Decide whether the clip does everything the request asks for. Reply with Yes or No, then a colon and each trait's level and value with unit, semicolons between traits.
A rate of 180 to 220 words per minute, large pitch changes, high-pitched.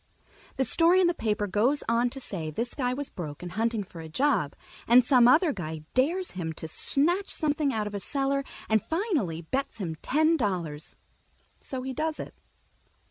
Yes: average, 190 wpm; wide, 7.8 semitones; high, 245 Hz